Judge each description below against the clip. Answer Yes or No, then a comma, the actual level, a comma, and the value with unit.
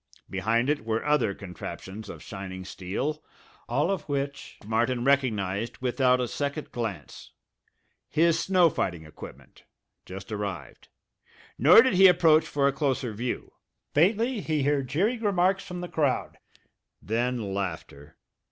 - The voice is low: Yes, low, 130 Hz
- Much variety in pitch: Yes, wide, 6.9 semitones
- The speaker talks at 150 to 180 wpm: No, slow, 135 wpm